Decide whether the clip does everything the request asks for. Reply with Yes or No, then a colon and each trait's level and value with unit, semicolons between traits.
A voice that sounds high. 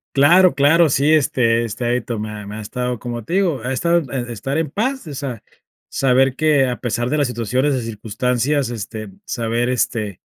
No: low, 125 Hz